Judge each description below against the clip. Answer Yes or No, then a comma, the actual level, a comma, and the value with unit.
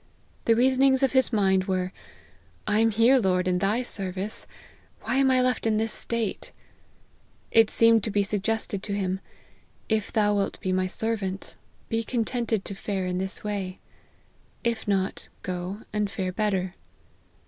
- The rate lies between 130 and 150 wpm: No, average, 160 wpm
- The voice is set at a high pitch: Yes, high, 210 Hz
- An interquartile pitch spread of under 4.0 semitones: Yes, average, 3.0 semitones